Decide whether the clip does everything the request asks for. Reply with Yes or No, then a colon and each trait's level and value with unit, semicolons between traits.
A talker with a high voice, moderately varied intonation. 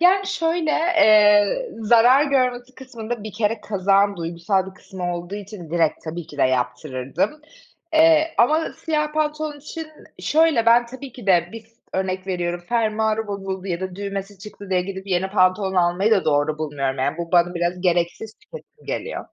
No: high, 200 Hz; wide, 6.2 semitones